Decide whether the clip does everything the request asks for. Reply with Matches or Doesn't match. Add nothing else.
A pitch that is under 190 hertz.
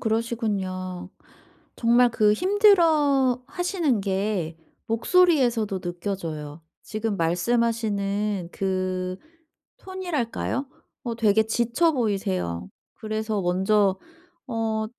Doesn't match